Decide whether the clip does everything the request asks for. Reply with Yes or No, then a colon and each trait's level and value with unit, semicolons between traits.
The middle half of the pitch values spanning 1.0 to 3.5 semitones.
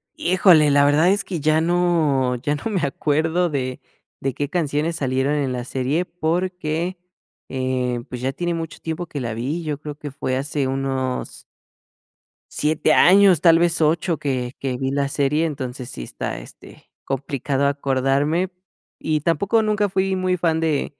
No: average, 4.0 semitones